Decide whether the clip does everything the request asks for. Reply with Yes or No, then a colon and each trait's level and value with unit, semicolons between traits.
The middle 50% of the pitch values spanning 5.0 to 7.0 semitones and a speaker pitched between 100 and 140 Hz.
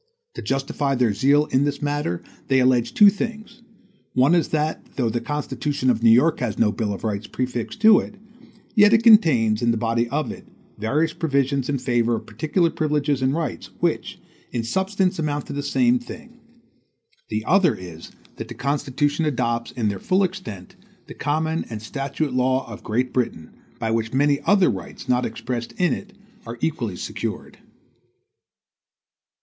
Yes: wide, 5.4 semitones; low, 135 Hz